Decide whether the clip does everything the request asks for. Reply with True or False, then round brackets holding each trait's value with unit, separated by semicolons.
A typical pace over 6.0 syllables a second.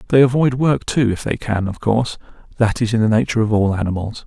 True (6.4 syllables/s)